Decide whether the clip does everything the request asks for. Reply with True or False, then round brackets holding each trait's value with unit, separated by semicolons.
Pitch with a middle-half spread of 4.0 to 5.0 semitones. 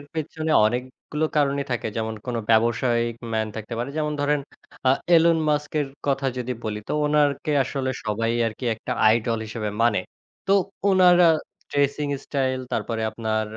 True (4.6 semitones)